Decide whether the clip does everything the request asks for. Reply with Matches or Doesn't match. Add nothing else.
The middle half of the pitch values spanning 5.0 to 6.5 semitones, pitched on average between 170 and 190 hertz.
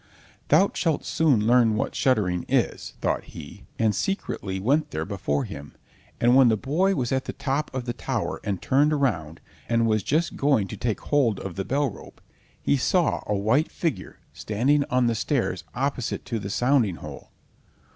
Doesn't match